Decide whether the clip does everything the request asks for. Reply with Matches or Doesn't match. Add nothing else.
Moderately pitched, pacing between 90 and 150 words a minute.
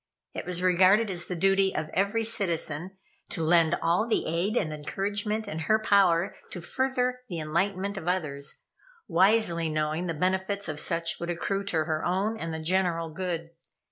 Doesn't match